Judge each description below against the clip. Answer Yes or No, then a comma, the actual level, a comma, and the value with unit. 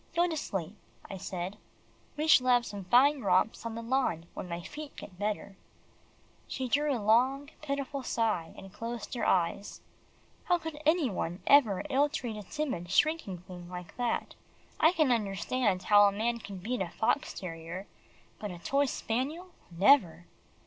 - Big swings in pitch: Yes, wide, 6.9 semitones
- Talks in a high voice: Yes, high, 225 Hz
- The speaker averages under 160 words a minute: No, average, 170 wpm